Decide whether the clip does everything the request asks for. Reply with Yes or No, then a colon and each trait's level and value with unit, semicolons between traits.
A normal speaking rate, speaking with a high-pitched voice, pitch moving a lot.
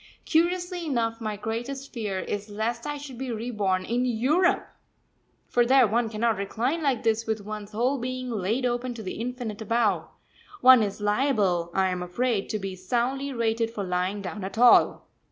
No: average, 175 wpm; high, 230 Hz; average, 3.5 semitones